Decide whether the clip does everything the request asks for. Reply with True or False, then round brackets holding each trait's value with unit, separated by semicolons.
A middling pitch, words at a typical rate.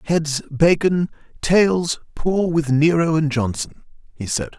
False (160 Hz; 105 wpm)